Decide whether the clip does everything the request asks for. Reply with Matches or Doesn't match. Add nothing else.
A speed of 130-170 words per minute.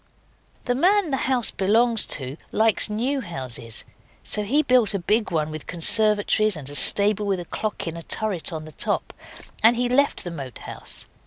Doesn't match